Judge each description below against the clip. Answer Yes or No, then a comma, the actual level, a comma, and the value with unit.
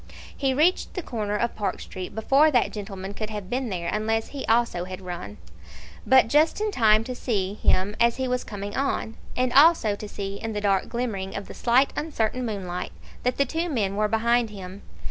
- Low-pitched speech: No, high, 220 Hz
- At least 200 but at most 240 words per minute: Yes, fast, 205 wpm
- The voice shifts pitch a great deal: No, average, 4.1 semitones